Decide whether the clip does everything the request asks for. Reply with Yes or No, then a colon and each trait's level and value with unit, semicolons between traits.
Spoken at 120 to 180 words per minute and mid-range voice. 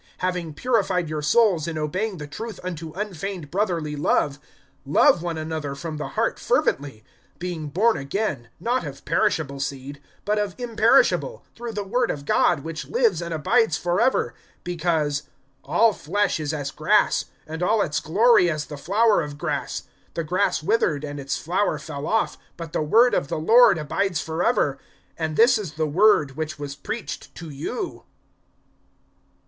Yes: average, 165 wpm; medium, 165 Hz